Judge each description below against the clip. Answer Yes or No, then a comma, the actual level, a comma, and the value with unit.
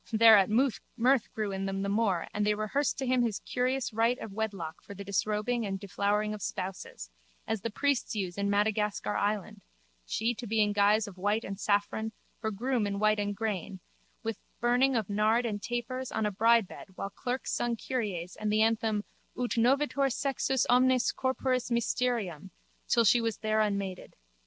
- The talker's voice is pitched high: Yes, high, 215 Hz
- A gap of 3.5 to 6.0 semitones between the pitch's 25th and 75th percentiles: No, average, 3.0 semitones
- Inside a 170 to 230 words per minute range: Yes, average, 180 wpm